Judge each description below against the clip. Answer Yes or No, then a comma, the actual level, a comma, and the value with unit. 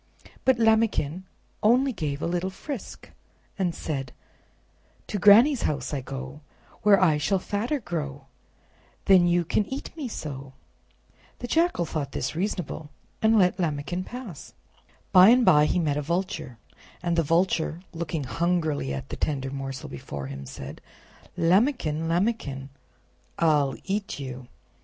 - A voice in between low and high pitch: Yes, medium, 170 Hz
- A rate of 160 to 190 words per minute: No, average, 140 wpm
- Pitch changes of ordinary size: No, wide, 6.0 semitones